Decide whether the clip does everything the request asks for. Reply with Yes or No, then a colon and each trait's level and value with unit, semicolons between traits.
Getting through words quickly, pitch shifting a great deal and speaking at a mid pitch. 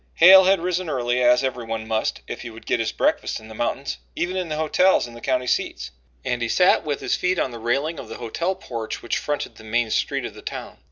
No: fast, 245 wpm; wide, 6.3 semitones; low, 125 Hz